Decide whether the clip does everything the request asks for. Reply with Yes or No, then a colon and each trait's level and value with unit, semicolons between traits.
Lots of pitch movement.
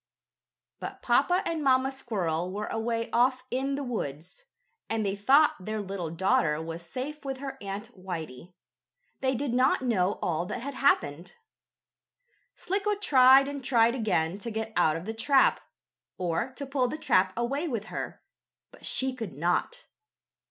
Yes: wide, 6.5 semitones